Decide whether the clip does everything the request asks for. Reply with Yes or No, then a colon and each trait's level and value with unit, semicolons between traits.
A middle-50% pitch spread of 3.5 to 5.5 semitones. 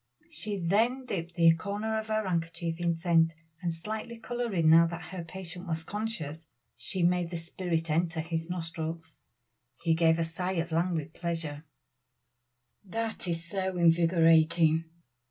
No: narrow, 2.4 semitones